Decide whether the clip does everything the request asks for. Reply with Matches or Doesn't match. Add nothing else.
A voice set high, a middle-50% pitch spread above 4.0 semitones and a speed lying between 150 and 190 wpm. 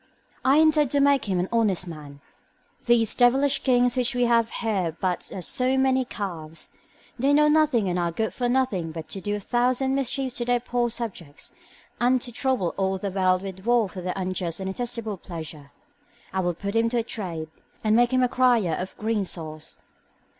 Doesn't match